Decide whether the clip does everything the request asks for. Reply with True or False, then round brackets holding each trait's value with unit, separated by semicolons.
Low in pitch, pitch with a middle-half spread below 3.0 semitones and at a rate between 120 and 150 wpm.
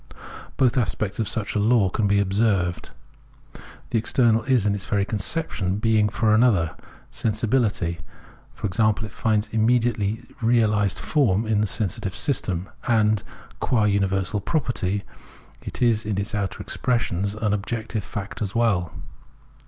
True (105 Hz; 2.4 semitones; 140 wpm)